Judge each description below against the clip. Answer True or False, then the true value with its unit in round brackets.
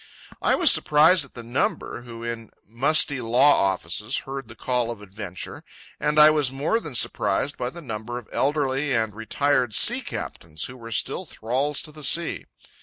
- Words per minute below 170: False (180 wpm)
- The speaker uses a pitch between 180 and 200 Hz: False (125 Hz)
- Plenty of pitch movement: False (4.3 semitones)